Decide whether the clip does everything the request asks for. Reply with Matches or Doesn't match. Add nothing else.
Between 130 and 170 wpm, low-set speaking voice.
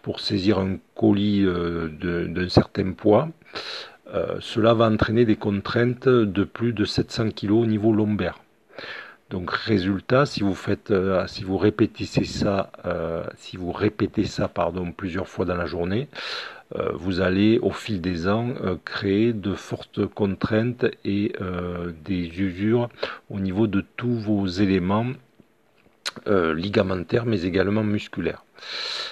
Matches